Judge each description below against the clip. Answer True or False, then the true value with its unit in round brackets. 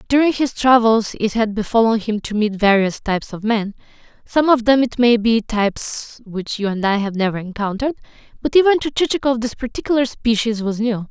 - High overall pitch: True (225 Hz)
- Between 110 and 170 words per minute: False (190 wpm)